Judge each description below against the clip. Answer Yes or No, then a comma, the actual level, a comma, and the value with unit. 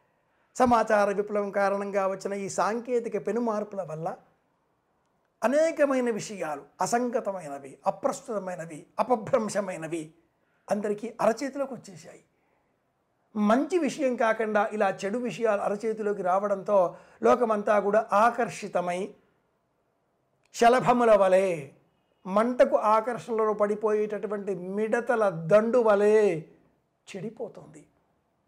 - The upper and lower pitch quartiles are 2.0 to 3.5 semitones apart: Yes, average, 3.2 semitones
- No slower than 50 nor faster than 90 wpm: Yes, average, 75 wpm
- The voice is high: Yes, high, 210 Hz